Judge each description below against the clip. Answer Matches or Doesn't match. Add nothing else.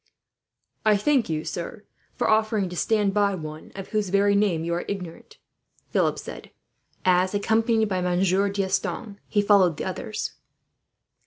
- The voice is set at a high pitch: Matches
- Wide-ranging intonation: Doesn't match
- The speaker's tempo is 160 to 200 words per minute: Doesn't match